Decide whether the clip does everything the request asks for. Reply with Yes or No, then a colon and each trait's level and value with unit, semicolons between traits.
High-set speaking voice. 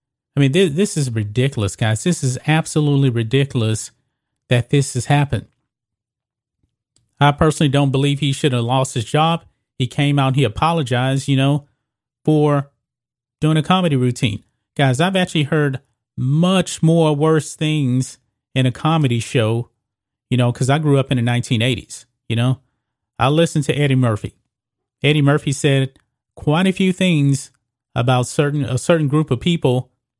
No: low, 135 Hz